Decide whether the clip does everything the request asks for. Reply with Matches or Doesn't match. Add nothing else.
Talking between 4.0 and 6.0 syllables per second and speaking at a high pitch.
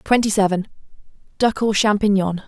Matches